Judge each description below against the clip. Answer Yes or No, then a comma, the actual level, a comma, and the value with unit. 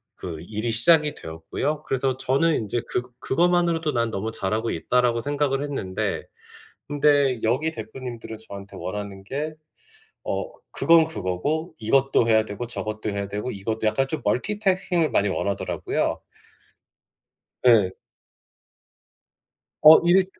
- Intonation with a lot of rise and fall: Yes, wide, 6.1 semitones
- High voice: No, low, 125 Hz